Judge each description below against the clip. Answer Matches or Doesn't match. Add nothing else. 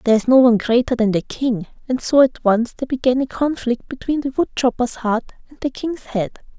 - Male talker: Doesn't match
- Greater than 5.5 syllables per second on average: Matches